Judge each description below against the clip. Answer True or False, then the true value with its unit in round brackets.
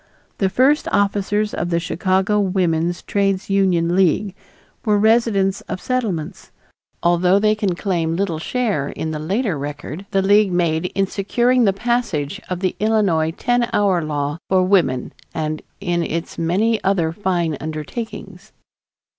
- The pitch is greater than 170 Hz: True (190 Hz)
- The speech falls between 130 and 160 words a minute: True (145 wpm)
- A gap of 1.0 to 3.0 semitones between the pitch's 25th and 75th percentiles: False (3.7 semitones)